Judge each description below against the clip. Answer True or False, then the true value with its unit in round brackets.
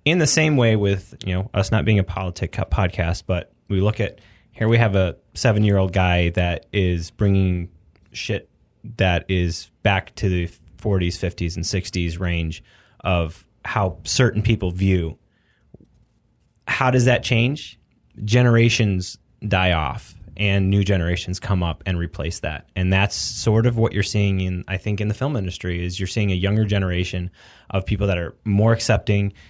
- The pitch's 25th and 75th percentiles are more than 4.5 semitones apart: False (3.3 semitones)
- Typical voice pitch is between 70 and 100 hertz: True (95 Hz)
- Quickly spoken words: False (170 wpm)